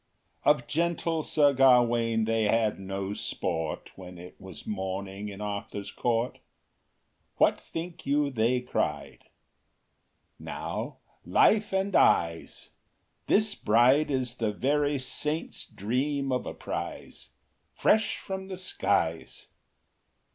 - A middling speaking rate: No, slow, 115 wpm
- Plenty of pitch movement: Yes, wide, 6.4 semitones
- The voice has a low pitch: Yes, low, 120 Hz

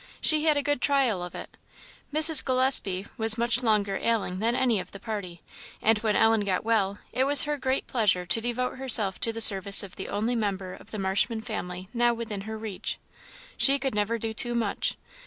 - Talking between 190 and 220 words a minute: Yes, average, 200 wpm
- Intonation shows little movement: No, average, 3.8 semitones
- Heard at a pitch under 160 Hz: No, high, 225 Hz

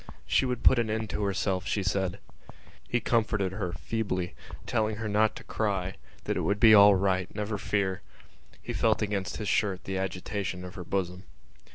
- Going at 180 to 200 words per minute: Yes, average, 185 wpm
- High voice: No, low, 100 Hz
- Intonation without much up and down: Yes, narrow, 2.3 semitones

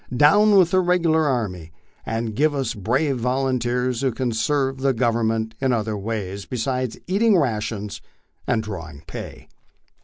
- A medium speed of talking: Yes, average, 150 wpm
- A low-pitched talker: Yes, low, 125 Hz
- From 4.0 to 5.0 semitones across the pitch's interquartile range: Yes, average, 4.3 semitones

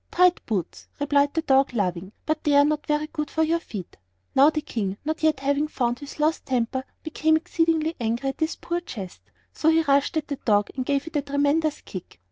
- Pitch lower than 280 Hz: No, very high, 285 Hz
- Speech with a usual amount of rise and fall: Yes, average, 3.6 semitones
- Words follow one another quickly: Yes, fast, 215 wpm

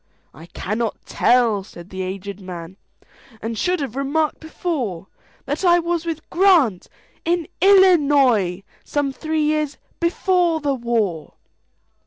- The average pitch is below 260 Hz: No, very high, 275 Hz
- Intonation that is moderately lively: No, wide, 8.6 semitones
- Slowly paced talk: Yes, slow, 105 wpm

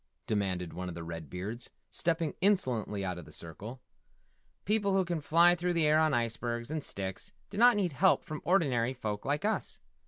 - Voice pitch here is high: No, low, 130 Hz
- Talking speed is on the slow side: No, average, 190 wpm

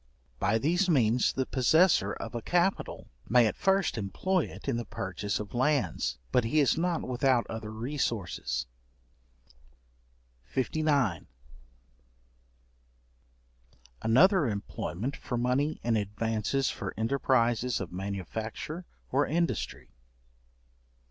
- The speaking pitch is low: Yes, low, 125 Hz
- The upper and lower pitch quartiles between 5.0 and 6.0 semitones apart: Yes, wide, 5.4 semitones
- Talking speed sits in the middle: No, slow, 110 wpm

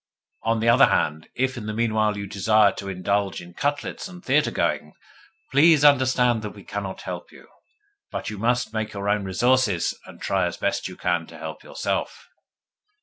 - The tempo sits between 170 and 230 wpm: Yes, average, 185 wpm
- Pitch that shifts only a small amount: No, average, 4.3 semitones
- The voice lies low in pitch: Yes, low, 110 Hz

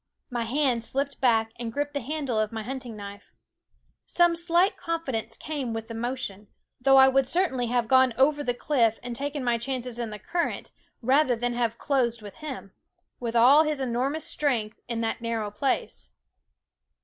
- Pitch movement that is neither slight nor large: Yes, average, 3.6 semitones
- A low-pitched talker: No, very high, 250 Hz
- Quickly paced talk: No, average, 180 wpm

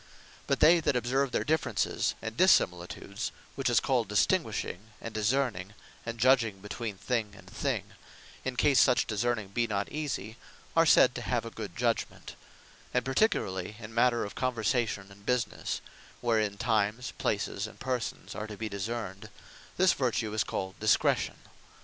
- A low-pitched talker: Yes, low, 115 Hz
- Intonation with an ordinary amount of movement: Yes, average, 3.4 semitones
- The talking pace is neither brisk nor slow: Yes, average, 155 wpm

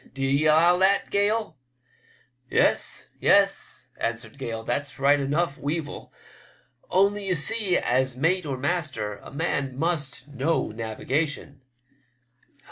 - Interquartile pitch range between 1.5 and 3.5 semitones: No, average, 4.8 semitones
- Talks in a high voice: No, medium, 145 Hz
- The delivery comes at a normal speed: No, slow, 120 wpm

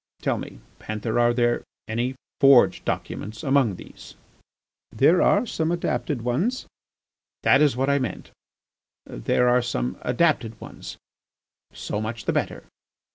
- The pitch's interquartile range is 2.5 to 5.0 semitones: Yes, average, 3.9 semitones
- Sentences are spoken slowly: Yes, slow, 130 wpm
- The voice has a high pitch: No, low, 125 Hz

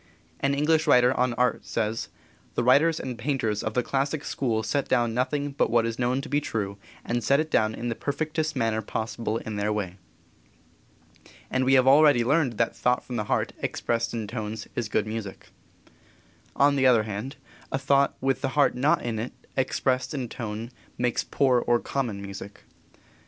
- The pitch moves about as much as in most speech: Yes, average, 3.7 semitones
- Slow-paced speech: No, average, 185 wpm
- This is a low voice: Yes, low, 125 Hz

